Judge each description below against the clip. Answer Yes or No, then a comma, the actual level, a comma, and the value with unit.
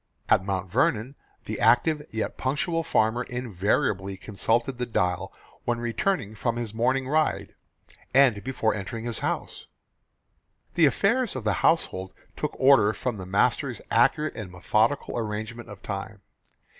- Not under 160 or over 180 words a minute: No, average, 140 wpm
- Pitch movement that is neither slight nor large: Yes, average, 4.3 semitones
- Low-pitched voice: Yes, low, 115 Hz